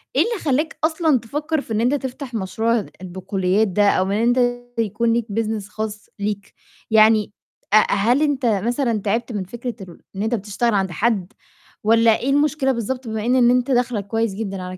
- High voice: Yes, high, 225 Hz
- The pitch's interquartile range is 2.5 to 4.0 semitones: Yes, average, 3.5 semitones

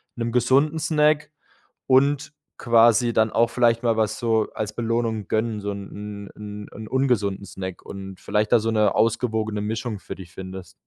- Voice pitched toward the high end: No, low, 110 Hz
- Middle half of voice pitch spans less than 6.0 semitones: Yes, narrow, 2.5 semitones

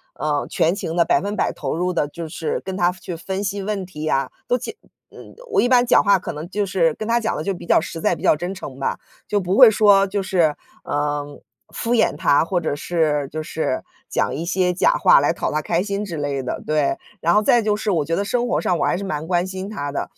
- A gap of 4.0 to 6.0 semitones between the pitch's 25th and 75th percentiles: Yes, average, 4.6 semitones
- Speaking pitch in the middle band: Yes, medium, 180 Hz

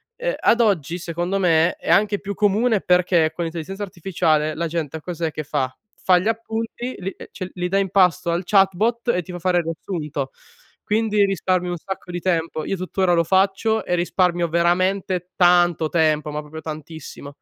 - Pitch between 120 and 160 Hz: No, medium, 180 Hz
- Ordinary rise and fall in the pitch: Yes, average, 3.0 semitones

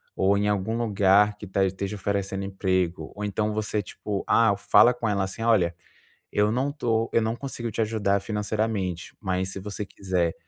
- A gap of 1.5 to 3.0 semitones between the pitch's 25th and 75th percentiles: Yes, narrow, 2.5 semitones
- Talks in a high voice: No, low, 105 Hz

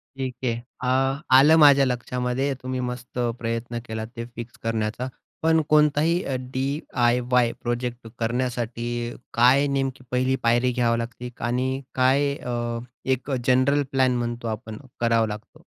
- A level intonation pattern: Yes, narrow, 2.1 semitones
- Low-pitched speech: Yes, low, 125 Hz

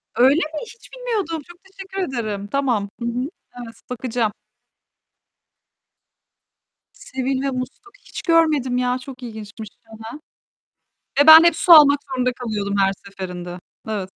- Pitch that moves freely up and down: Yes, wide, 6.1 semitones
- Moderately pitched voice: No, very high, 255 Hz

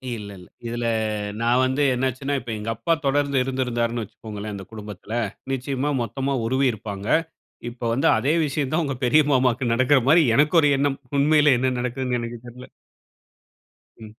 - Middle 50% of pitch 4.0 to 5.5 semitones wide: No, average, 3.1 semitones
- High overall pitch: No, low, 125 Hz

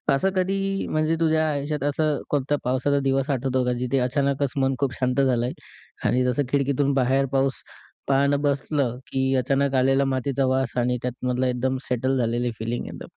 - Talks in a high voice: No, low, 135 Hz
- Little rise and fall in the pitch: Yes, narrow, 1.9 semitones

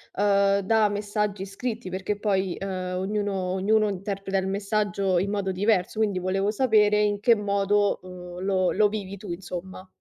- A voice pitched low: No, high, 200 Hz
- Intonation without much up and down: Yes, narrow, 1.7 semitones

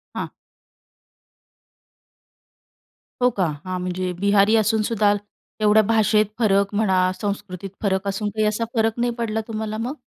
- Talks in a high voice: Yes, high, 210 Hz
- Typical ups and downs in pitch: No, narrow, 1.9 semitones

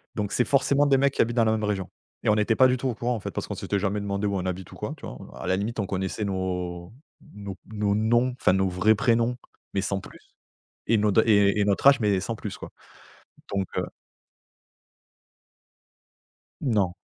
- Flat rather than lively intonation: No, average, 3.2 semitones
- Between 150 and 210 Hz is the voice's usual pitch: No, low, 105 Hz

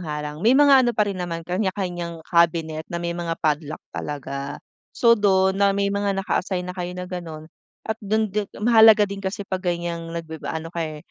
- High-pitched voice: No, medium, 175 Hz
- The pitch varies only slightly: No, average, 3.5 semitones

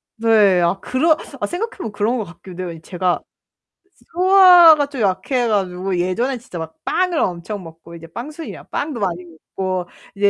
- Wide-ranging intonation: Yes, wide, 7.8 semitones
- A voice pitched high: Yes, high, 205 Hz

